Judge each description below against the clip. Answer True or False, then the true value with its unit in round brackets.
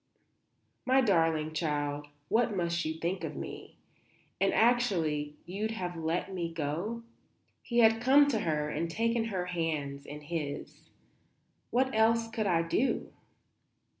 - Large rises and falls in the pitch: True (6.2 semitones)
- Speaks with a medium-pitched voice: True (175 Hz)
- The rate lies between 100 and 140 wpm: True (135 wpm)